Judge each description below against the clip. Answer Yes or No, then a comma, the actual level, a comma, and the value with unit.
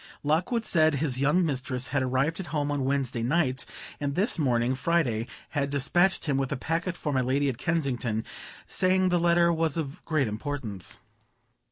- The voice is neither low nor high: Yes, medium, 145 Hz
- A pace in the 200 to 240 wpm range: No, average, 175 wpm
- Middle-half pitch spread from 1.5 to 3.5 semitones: No, average, 4.3 semitones